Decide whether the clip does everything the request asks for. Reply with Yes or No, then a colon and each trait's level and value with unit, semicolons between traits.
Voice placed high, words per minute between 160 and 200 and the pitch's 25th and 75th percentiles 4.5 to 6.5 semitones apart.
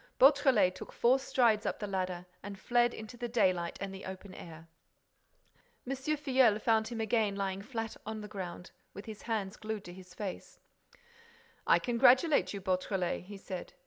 No: high, 210 Hz; average, 170 wpm; average, 4.1 semitones